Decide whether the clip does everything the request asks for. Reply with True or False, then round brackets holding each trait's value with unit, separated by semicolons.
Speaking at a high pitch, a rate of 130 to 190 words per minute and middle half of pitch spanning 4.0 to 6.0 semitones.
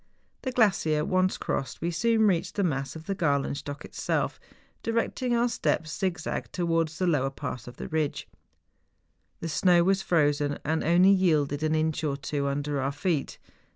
False (160 Hz; 175 wpm; 4.3 semitones)